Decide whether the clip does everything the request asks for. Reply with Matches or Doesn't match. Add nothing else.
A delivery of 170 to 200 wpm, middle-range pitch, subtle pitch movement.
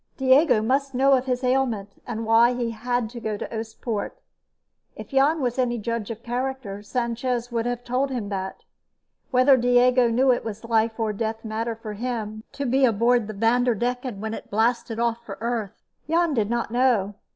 Doesn't match